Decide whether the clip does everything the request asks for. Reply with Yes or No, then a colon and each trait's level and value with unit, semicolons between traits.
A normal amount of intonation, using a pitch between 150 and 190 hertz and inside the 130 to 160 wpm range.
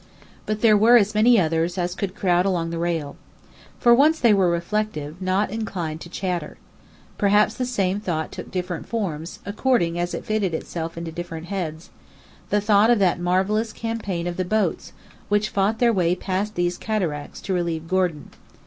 No: average, 3.8 semitones; medium, 185 Hz; average, 175 wpm